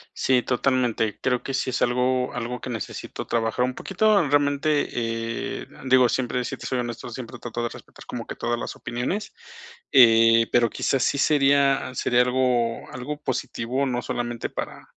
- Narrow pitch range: Yes, narrow, 2.0 semitones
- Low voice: Yes, low, 125 Hz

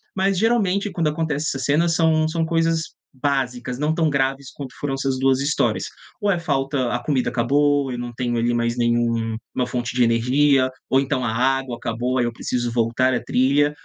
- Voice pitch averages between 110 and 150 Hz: Yes, low, 135 Hz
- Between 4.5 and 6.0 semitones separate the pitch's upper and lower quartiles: No, average, 3.5 semitones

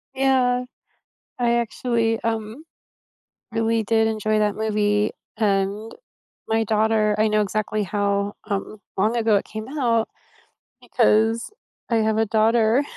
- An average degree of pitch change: No, narrow, 1.3 semitones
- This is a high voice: Yes, high, 220 Hz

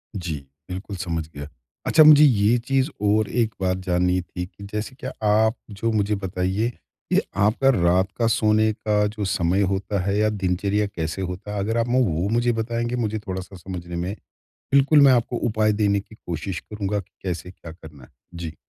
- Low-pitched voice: Yes, low, 100 Hz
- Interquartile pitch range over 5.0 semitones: No, average, 3.4 semitones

